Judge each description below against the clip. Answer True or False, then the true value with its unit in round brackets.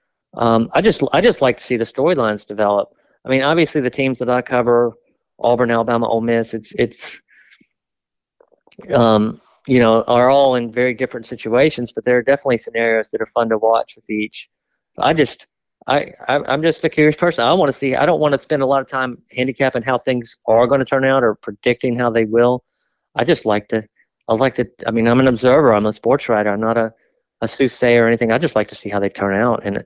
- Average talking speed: False (225 wpm)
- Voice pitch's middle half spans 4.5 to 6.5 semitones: False (2.7 semitones)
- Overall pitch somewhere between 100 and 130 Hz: True (120 Hz)